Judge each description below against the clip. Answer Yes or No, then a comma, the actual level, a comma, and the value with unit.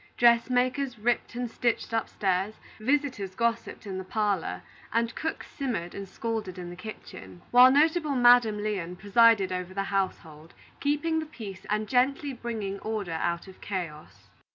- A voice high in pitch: Yes, high, 215 Hz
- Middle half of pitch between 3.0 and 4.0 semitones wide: No, average, 4.7 semitones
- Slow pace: No, average, 150 wpm